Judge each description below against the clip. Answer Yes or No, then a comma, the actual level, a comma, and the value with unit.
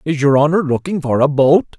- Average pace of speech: No, fast, 235 wpm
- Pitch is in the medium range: Yes, medium, 150 Hz